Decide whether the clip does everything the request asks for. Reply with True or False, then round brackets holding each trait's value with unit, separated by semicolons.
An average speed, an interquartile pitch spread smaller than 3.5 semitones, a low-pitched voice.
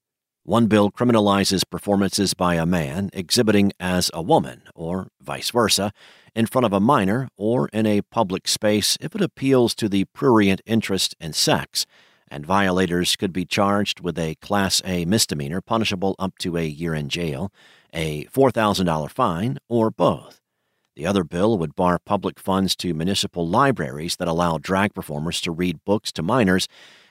True (165 wpm; 3.0 semitones; 95 Hz)